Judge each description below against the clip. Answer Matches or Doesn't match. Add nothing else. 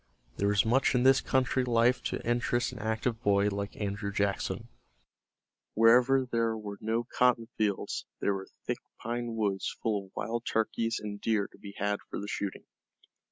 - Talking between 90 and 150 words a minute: Doesn't match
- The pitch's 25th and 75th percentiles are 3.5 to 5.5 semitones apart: Doesn't match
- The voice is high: Doesn't match